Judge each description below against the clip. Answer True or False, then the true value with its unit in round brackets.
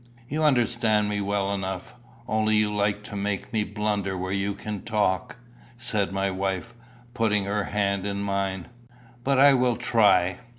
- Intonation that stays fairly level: True (1.8 semitones)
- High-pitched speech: False (105 Hz)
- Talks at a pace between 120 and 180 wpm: True (160 wpm)